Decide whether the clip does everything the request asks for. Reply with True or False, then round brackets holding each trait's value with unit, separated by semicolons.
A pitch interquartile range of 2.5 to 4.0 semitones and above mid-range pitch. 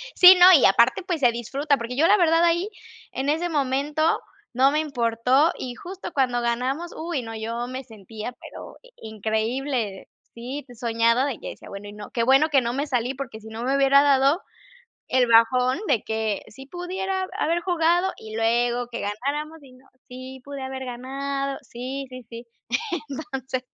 True (3.7 semitones; 260 Hz)